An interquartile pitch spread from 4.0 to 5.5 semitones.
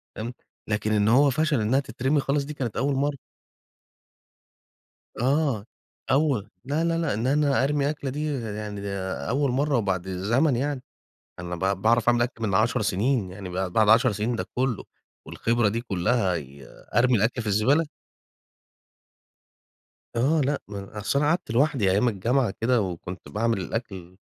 Yes: average, 5.2 semitones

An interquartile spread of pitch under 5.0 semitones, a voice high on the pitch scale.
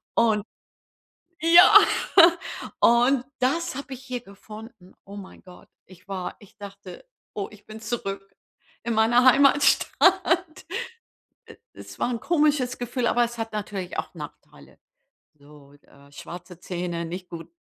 No: wide, 5.4 semitones; high, 220 Hz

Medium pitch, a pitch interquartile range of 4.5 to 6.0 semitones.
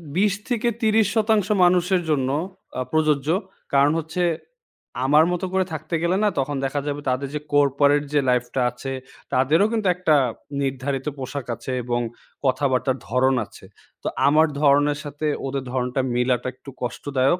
Yes: medium, 145 Hz; average, 5.0 semitones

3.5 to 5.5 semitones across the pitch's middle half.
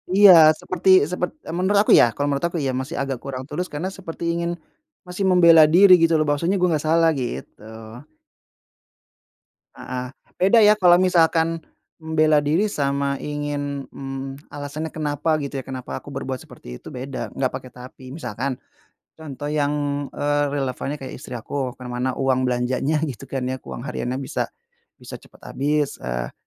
Yes: average, 3.9 semitones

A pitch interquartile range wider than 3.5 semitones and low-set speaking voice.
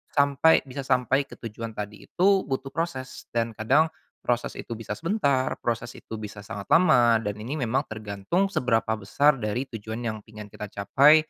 Yes: average, 4.5 semitones; low, 120 Hz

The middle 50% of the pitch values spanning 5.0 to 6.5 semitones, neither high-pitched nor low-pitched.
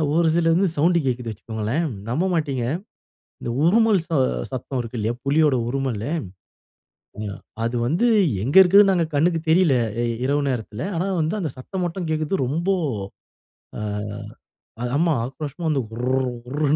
Yes: wide, 5.5 semitones; medium, 145 Hz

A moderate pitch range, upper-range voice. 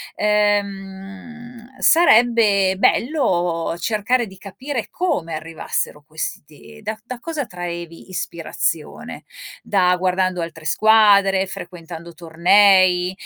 Yes: average, 4.0 semitones; high, 195 Hz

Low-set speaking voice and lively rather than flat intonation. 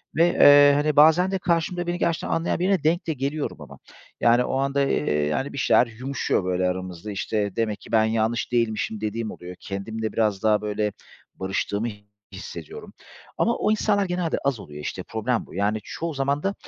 Yes: low, 120 Hz; wide, 6.9 semitones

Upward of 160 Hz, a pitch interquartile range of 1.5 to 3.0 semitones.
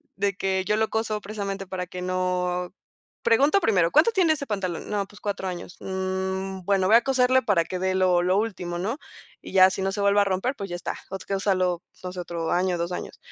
Yes: high, 190 Hz; narrow, 2.4 semitones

